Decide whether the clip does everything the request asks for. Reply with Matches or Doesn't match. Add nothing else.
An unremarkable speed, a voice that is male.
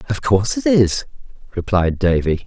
Matches